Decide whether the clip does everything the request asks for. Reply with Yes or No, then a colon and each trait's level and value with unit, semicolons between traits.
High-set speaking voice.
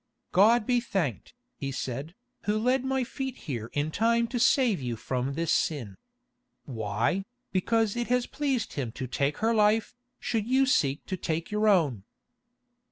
Yes: high, 195 Hz